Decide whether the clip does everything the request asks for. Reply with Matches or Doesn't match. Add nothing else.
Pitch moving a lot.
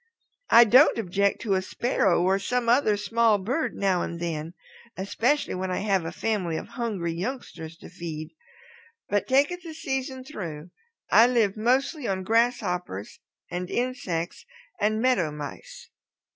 Matches